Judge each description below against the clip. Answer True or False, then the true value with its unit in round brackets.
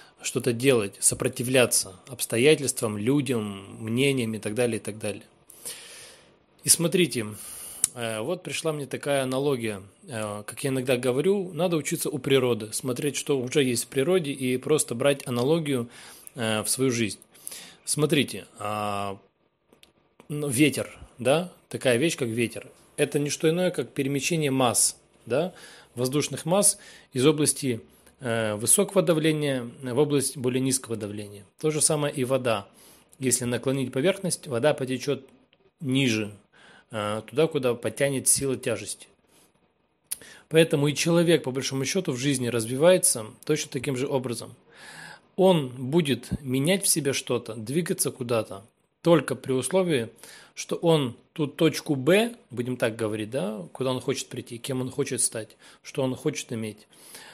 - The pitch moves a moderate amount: True (4.1 semitones)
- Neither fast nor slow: True (135 wpm)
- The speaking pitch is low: True (130 Hz)